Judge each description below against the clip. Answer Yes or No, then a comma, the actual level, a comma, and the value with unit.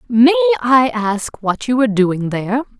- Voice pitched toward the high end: Yes, high, 225 Hz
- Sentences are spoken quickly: No, average, 170 wpm